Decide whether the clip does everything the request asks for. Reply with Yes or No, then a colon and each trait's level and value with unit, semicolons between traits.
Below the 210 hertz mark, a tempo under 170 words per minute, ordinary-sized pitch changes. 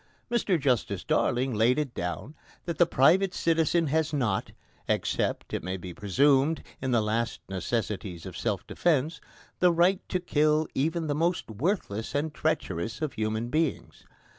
No: medium, 140 Hz; average, 155 wpm; wide, 6.9 semitones